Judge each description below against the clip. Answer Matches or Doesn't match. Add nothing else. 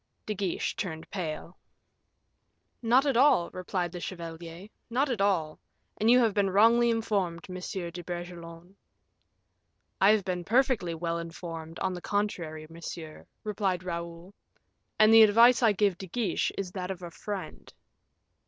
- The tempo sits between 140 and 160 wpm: Matches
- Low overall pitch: Doesn't match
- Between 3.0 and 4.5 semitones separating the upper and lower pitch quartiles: Matches